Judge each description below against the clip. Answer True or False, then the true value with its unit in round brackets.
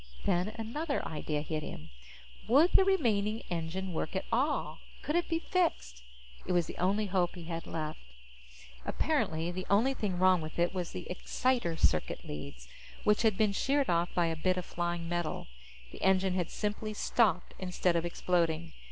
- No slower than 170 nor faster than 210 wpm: True (175 wpm)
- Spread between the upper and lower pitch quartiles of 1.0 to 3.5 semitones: False (4.3 semitones)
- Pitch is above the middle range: False (180 Hz)